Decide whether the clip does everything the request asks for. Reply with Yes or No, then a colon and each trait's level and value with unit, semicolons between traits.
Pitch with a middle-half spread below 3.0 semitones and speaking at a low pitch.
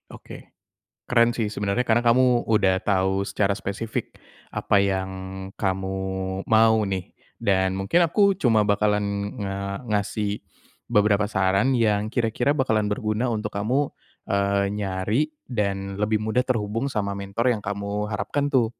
Yes: narrow, 2.6 semitones; low, 105 Hz